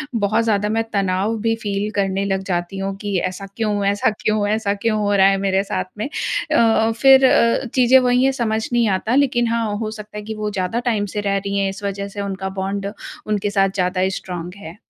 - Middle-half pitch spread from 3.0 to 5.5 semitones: No, narrow, 2.4 semitones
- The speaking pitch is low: No, high, 205 Hz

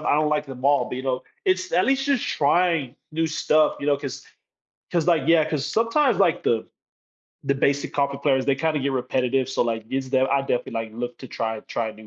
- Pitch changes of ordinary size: Yes, average, 3.6 semitones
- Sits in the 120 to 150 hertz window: Yes, medium, 140 Hz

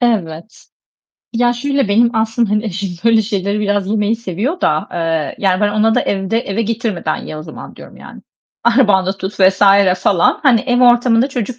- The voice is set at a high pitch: Yes, high, 215 Hz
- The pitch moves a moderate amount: Yes, average, 3.6 semitones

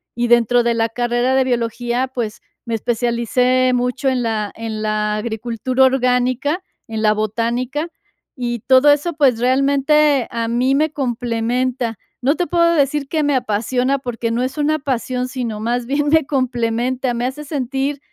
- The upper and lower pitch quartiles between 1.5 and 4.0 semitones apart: Yes, narrow, 2.6 semitones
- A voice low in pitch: No, very high, 250 Hz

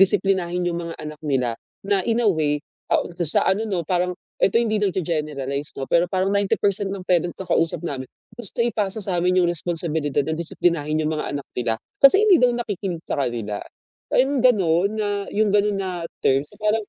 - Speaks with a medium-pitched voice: Yes, medium, 180 Hz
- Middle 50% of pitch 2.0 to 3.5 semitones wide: No, average, 4.8 semitones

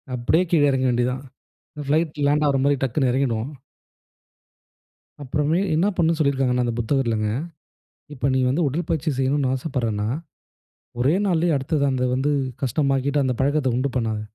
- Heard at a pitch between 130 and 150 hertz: Yes, low, 135 Hz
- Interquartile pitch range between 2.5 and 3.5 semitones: Yes, average, 2.9 semitones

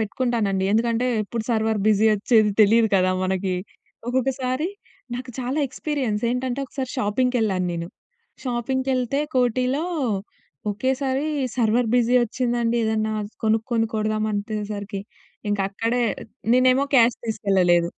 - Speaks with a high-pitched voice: Yes, high, 230 Hz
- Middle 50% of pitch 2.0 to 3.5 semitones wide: Yes, average, 3.2 semitones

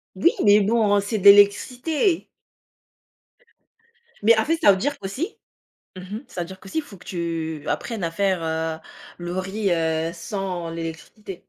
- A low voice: No, high, 195 Hz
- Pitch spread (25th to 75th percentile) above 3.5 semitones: Yes, average, 4.2 semitones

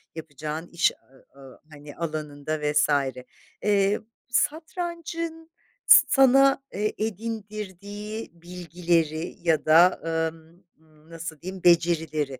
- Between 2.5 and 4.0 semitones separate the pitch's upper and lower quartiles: No, average, 5.3 semitones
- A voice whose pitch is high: No, medium, 175 Hz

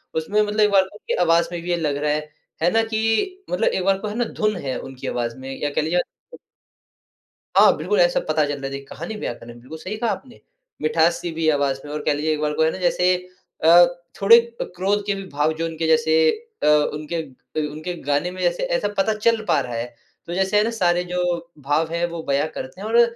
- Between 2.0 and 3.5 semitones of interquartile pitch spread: No, average, 4.5 semitones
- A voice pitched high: No, medium, 170 Hz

